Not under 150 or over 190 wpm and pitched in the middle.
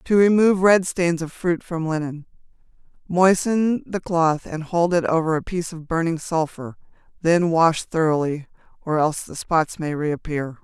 Yes: average, 160 wpm; medium, 165 Hz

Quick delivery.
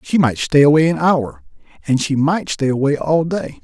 Yes: fast, 215 wpm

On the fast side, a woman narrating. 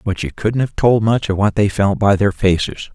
No: fast, 265 wpm; male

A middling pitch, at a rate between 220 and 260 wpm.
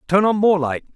Yes: medium, 180 Hz; fast, 255 wpm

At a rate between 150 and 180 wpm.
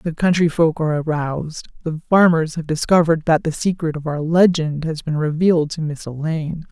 No: average, 190 wpm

